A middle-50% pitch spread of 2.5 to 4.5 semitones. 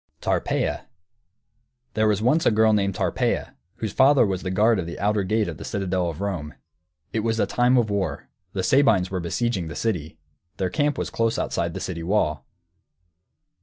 Yes: average, 3.7 semitones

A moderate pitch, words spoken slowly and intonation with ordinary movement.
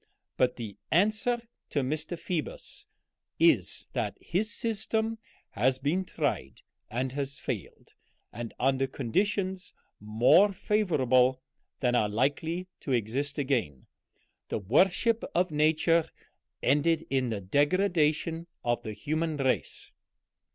No: medium, 145 Hz; slow, 115 wpm; wide, 6.0 semitones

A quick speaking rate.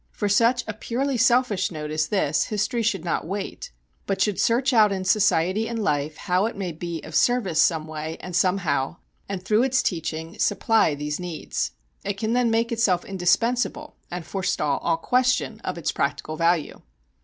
No: average, 180 wpm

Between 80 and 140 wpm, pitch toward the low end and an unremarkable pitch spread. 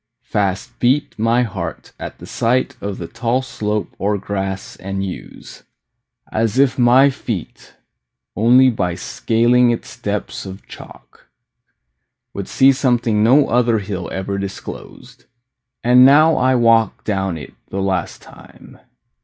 Yes: slow, 135 wpm; low, 115 Hz; average, 4.2 semitones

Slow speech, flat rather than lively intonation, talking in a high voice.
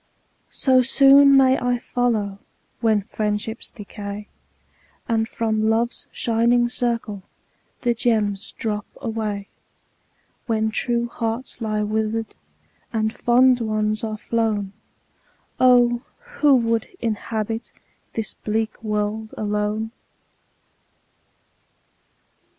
Yes: slow, 95 wpm; narrow, 2.1 semitones; high, 225 Hz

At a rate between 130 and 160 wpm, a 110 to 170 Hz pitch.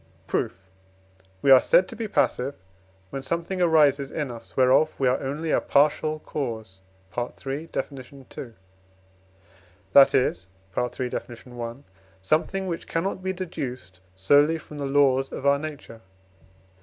Yes: average, 140 wpm; medium, 140 Hz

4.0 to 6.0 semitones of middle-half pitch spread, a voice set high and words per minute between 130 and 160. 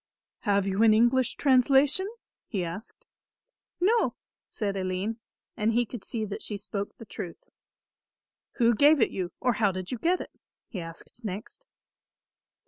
Yes: average, 4.6 semitones; high, 220 Hz; average, 150 wpm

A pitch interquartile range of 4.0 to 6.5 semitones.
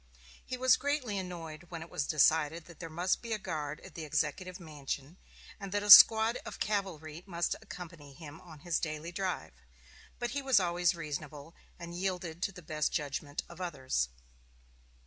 No: average, 3.6 semitones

